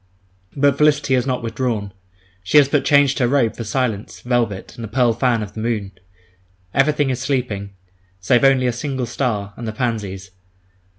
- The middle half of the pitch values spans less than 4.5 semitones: Yes, average, 3.7 semitones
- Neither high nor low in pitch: No, low, 120 Hz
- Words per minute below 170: No, average, 175 wpm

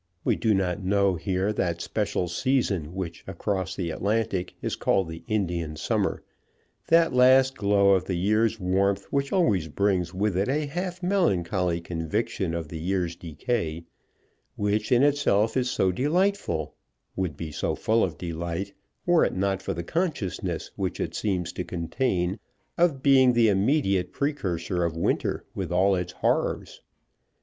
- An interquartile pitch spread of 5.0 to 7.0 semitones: Yes, wide, 5.4 semitones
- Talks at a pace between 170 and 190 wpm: No, average, 155 wpm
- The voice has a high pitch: No, very low, 95 Hz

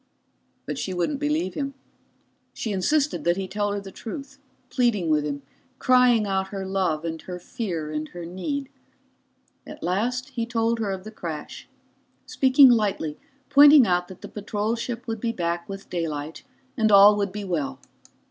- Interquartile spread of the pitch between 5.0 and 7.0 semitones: Yes, average, 5.3 semitones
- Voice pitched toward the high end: Yes, high, 200 Hz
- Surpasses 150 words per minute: Yes, average, 170 wpm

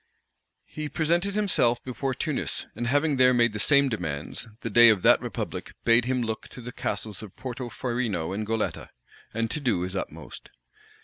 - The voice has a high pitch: No, low, 120 Hz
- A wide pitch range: No, average, 3.9 semitones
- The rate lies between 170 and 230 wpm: Yes, average, 175 wpm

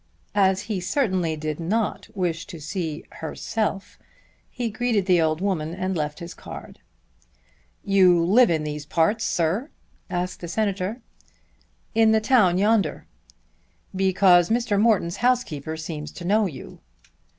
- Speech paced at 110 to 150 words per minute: Yes, slow, 135 wpm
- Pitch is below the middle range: No, medium, 185 Hz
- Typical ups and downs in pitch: Yes, average, 4.5 semitones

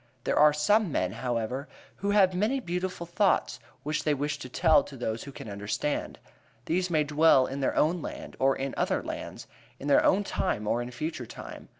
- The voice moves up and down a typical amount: No, wide, 5.8 semitones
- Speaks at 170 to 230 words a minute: Yes, average, 200 wpm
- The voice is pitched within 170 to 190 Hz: No, medium, 150 Hz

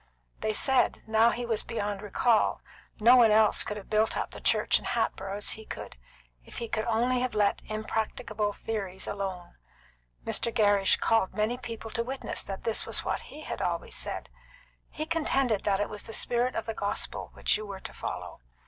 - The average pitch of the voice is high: Yes, high, 220 Hz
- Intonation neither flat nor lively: No, narrow, 2.3 semitones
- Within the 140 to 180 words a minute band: No, average, 195 wpm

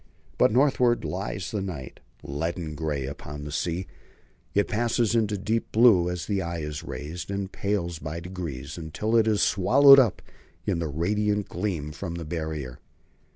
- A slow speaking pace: No, average, 160 wpm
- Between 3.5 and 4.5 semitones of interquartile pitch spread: No, average, 5.0 semitones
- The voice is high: No, very low, 90 Hz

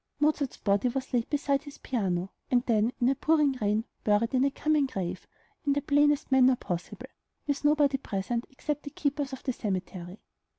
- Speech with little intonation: No, average, 5.3 semitones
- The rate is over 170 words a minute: Yes, average, 180 wpm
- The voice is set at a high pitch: Yes, very high, 260 Hz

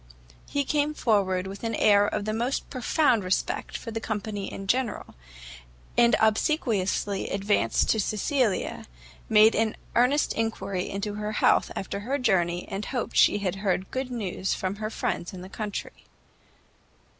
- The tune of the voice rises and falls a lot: No, average, 3.3 semitones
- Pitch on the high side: Yes, high, 210 Hz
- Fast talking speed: No, average, 155 wpm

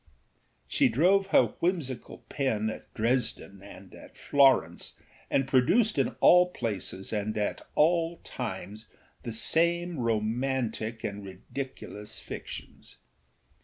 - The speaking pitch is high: No, low, 125 Hz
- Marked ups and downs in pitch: Yes, wide, 6.9 semitones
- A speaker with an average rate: No, slow, 110 wpm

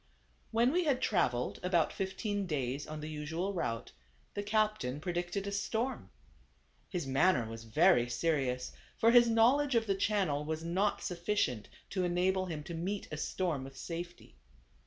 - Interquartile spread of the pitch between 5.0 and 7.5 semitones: Yes, average, 5.3 semitones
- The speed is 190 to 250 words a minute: No, average, 155 wpm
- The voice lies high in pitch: No, medium, 175 Hz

